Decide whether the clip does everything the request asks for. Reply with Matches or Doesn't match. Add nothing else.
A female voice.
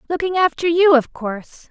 Matches